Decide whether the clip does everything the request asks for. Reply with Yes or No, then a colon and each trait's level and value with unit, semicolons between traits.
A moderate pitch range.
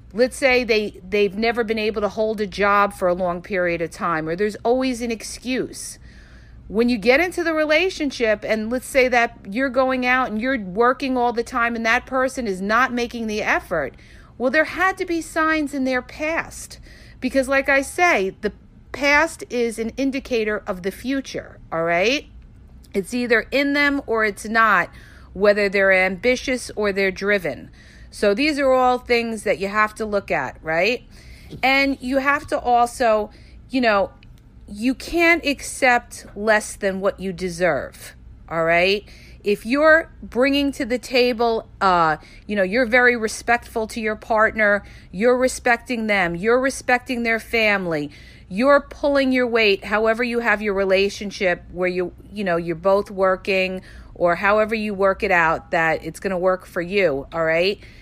Yes: average, 4.5 semitones